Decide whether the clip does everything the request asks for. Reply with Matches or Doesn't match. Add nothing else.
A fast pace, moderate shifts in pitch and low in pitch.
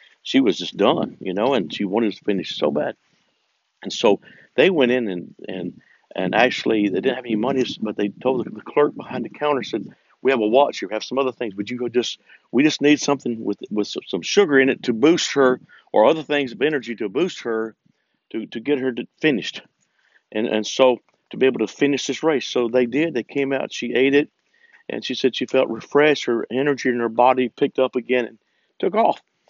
Matches